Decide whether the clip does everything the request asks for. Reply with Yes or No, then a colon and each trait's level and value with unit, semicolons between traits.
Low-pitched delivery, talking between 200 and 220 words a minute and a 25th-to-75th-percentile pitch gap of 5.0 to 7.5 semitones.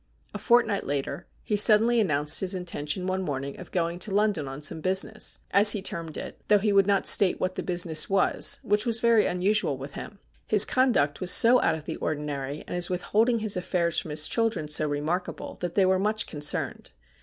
No: medium, 185 Hz; fast, 205 wpm; average, 5.3 semitones